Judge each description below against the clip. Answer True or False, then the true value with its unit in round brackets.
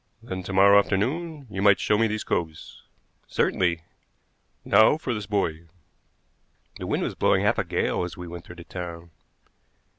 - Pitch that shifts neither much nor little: True (3.6 semitones)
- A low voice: True (95 Hz)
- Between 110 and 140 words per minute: False (170 wpm)